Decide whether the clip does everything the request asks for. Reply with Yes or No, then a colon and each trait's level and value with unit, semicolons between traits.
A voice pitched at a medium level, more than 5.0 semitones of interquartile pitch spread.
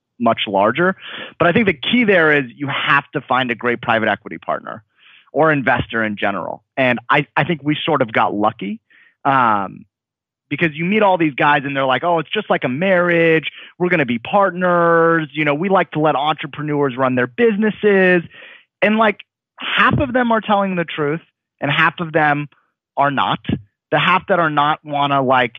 Yes: medium, 150 Hz; wide, 5.5 semitones